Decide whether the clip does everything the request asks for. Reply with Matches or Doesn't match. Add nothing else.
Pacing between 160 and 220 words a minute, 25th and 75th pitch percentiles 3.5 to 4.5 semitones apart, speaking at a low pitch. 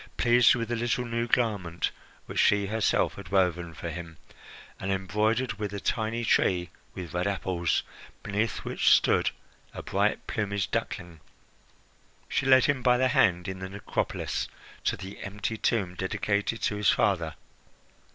Doesn't match